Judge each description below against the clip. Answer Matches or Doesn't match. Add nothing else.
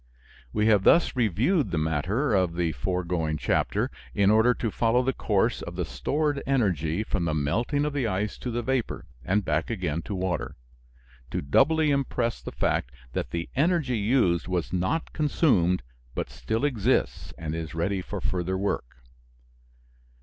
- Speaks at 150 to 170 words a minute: Matches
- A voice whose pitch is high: Doesn't match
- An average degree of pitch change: Doesn't match